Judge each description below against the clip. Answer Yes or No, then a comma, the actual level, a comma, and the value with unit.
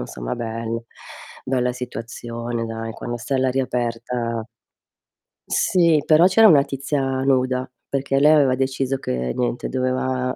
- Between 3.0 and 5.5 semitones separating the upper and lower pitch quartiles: No, narrow, 2.6 semitones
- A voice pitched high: No, low, 130 Hz